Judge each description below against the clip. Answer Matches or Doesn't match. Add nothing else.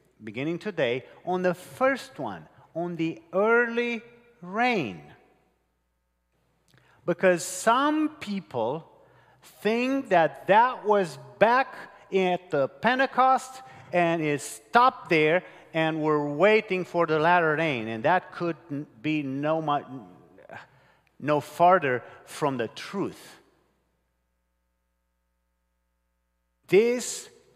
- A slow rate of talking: Matches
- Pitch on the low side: Doesn't match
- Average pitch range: Doesn't match